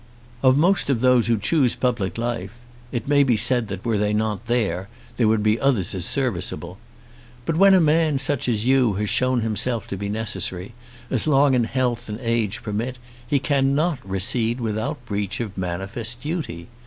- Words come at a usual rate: Yes, average, 180 wpm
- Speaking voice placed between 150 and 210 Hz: No, low, 115 Hz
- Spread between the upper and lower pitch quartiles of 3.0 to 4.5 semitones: Yes, average, 3.9 semitones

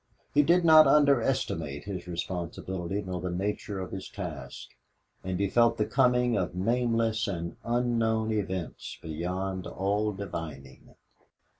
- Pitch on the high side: No, low, 100 Hz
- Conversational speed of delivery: No, slow, 130 wpm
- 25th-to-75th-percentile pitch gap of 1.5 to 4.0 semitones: No, average, 4.6 semitones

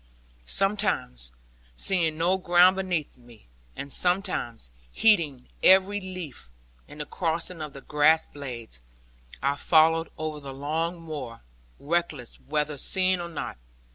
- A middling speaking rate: No, slow, 125 wpm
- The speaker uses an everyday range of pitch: Yes, average, 4.4 semitones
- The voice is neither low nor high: Yes, medium, 155 Hz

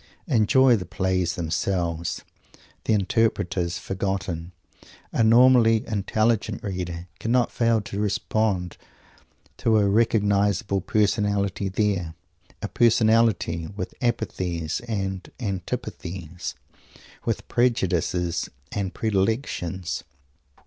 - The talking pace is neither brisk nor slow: No, slow, 85 wpm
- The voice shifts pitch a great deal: No, average, 3.8 semitones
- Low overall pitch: Yes, low, 100 Hz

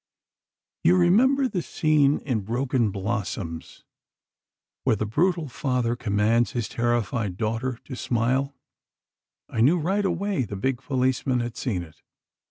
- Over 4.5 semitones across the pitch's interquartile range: Yes, average, 5.0 semitones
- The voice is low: Yes, low, 125 Hz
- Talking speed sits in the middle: No, slow, 130 wpm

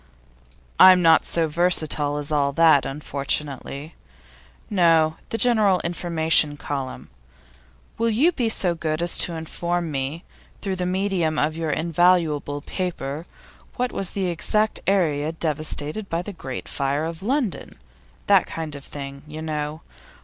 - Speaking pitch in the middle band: Yes, medium, 160 Hz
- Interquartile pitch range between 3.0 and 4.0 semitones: Yes, average, 3.5 semitones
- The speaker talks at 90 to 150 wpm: Yes, average, 140 wpm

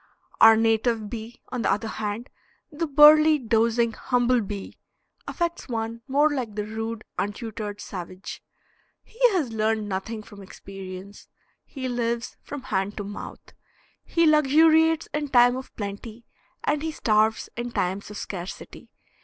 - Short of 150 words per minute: Yes, average, 140 wpm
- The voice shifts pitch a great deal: No, average, 4.2 semitones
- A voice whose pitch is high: Yes, high, 230 Hz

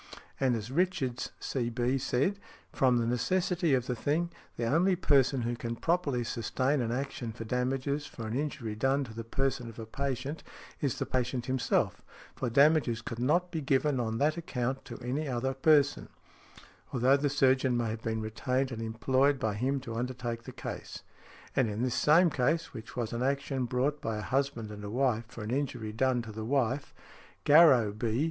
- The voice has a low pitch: Yes, low, 130 Hz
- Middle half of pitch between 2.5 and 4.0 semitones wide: Yes, average, 3.1 semitones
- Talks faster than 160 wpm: Yes, average, 190 wpm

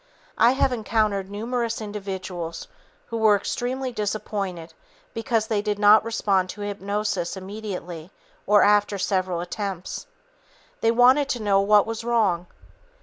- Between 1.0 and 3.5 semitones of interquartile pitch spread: Yes, average, 2.8 semitones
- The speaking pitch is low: No, high, 205 Hz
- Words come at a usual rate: No, slow, 130 wpm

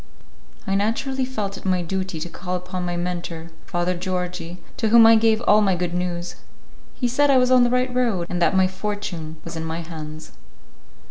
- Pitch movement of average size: Yes, average, 4.3 semitones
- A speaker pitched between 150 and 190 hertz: Yes, medium, 185 Hz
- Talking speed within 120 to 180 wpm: No, average, 200 wpm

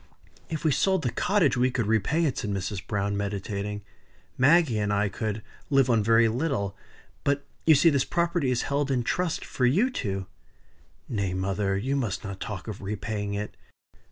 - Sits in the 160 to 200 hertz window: No, low, 115 Hz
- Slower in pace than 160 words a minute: No, average, 180 wpm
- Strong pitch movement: Yes, wide, 5.7 semitones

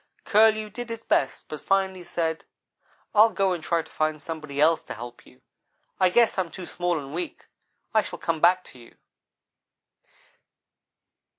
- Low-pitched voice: No, medium, 175 Hz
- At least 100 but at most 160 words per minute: No, average, 170 wpm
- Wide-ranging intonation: No, average, 4.1 semitones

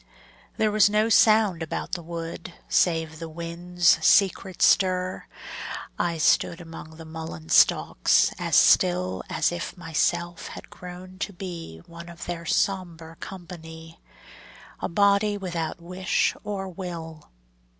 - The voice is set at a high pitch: No, medium, 170 Hz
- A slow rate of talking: Yes, slow, 130 wpm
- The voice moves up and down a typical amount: No, narrow, 2.3 semitones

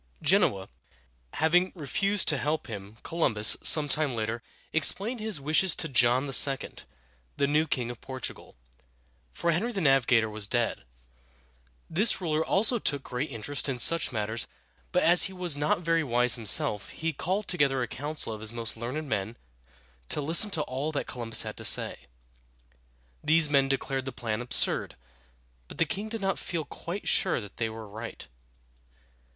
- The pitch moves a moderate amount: No, wide, 5.9 semitones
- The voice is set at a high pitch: No, medium, 140 Hz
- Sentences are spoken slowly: No, average, 165 wpm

